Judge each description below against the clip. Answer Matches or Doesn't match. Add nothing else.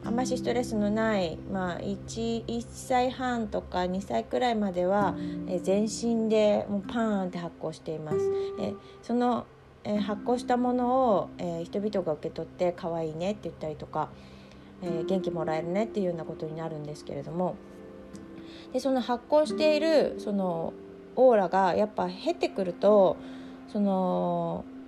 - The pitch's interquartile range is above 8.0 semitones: Doesn't match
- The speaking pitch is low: Doesn't match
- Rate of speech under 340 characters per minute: Matches